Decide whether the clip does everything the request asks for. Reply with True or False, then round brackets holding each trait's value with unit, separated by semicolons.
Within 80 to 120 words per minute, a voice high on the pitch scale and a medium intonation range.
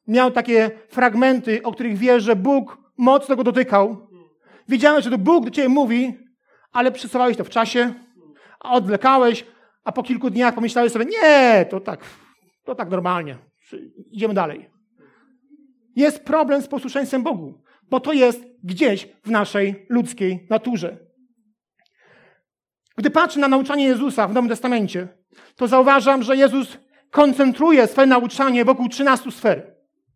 False (140 wpm; 245 Hz; 3.5 semitones)